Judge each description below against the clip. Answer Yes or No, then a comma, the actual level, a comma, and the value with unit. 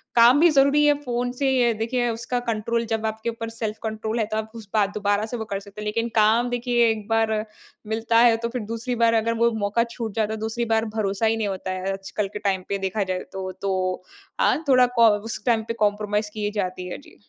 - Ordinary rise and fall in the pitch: No, narrow, 2.0 semitones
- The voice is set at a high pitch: Yes, high, 220 Hz